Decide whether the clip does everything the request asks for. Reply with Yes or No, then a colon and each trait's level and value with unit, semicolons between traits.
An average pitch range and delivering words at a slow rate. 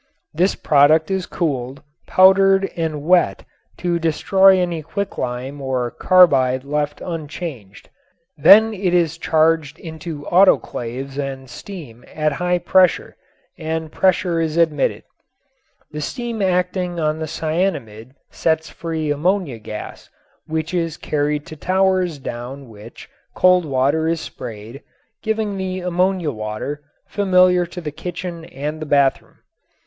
Yes: average, 4.3 semitones; slow, 125 wpm